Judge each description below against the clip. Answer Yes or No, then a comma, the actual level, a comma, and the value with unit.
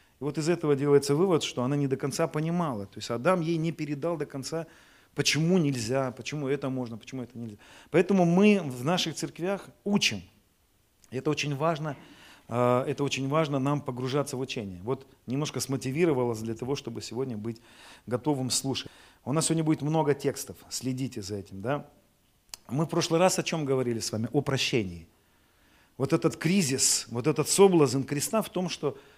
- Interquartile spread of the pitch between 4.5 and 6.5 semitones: Yes, average, 4.8 semitones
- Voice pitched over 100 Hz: Yes, medium, 140 Hz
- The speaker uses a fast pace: Yes, fast, 175 wpm